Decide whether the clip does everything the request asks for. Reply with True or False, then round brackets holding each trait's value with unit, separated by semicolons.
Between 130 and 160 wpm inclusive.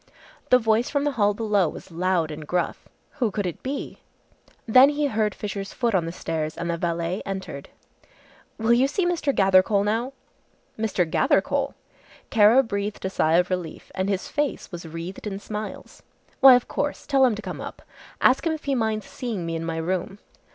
False (190 wpm)